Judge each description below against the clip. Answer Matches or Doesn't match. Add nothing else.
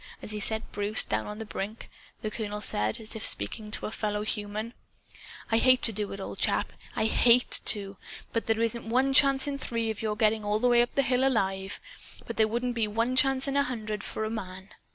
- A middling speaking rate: Doesn't match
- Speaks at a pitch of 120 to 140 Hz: Doesn't match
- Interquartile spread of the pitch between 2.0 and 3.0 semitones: Matches